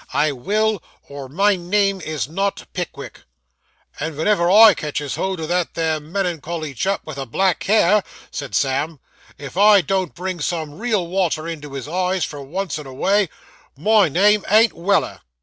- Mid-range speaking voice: Yes, medium, 175 Hz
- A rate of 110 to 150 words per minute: No, average, 170 wpm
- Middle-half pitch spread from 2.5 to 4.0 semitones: No, average, 4.6 semitones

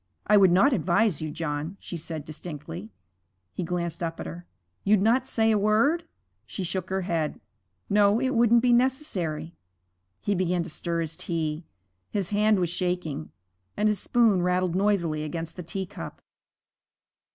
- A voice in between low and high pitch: Yes, medium, 180 Hz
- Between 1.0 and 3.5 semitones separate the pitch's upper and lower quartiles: No, average, 4.3 semitones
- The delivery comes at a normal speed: Yes, average, 160 wpm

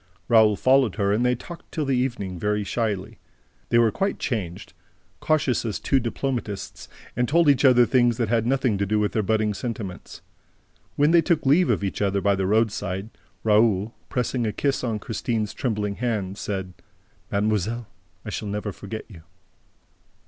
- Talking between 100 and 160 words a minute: No, average, 170 wpm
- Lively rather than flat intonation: No, average, 3.5 semitones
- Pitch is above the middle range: No, low, 110 Hz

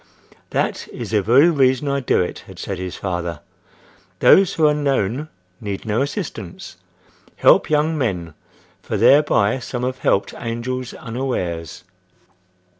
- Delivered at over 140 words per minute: No, slow, 135 wpm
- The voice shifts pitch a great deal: Yes, wide, 6.0 semitones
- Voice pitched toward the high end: No, low, 120 Hz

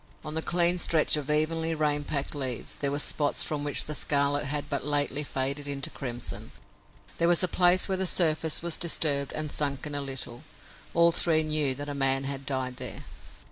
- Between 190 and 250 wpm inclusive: Yes, average, 195 wpm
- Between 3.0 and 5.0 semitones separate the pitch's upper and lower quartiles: No, narrow, 2.4 semitones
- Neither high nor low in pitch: Yes, medium, 145 Hz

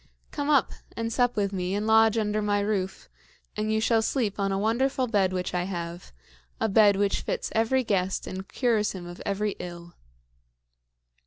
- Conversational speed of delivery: Yes, average, 180 wpm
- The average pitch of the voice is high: Yes, high, 210 Hz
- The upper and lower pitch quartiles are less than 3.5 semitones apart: Yes, average, 2.8 semitones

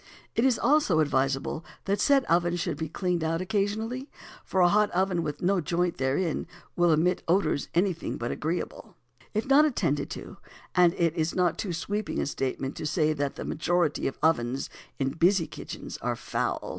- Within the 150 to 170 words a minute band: No, average, 180 wpm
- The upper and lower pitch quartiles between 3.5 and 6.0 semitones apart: Yes, average, 4.2 semitones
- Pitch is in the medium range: Yes, medium, 175 Hz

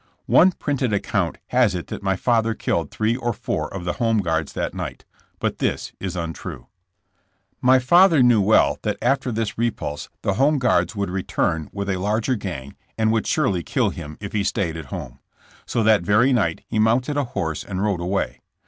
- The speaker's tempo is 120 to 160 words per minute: No, average, 195 wpm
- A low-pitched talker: Yes, low, 105 Hz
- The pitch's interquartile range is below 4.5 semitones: No, average, 4.9 semitones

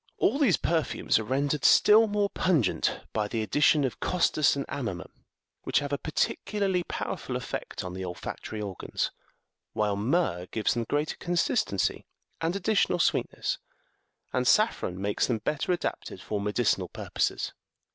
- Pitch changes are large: Yes, wide, 8.9 semitones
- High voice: No, medium, 140 Hz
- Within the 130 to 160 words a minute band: Yes, average, 150 wpm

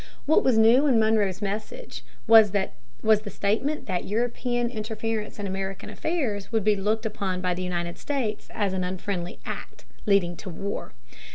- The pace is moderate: Yes, average, 160 wpm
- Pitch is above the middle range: Yes, high, 210 Hz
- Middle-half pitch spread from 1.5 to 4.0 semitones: Yes, average, 2.8 semitones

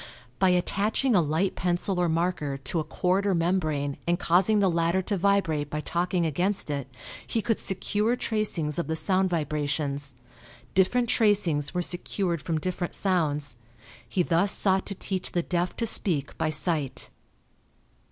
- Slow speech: No, average, 160 wpm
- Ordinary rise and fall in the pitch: Yes, average, 3.7 semitones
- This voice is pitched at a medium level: Yes, medium, 175 Hz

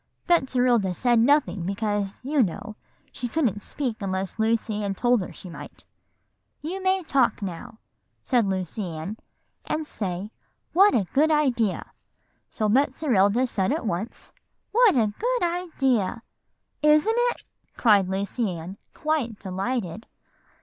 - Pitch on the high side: Yes, high, 230 Hz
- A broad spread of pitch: Yes, wide, 6.7 semitones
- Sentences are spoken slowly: Yes, slow, 130 wpm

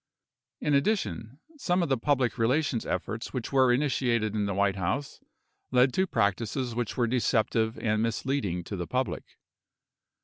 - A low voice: Yes, low, 120 Hz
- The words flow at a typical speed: Yes, average, 160 wpm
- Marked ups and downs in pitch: No, average, 3.8 semitones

